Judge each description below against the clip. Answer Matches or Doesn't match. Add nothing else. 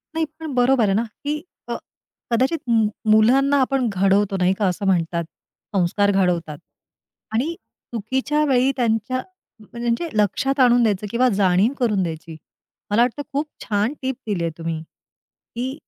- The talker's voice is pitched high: Matches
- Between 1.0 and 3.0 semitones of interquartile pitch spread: Doesn't match